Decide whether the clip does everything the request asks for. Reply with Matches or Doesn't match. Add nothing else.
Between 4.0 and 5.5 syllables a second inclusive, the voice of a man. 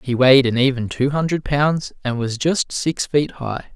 Matches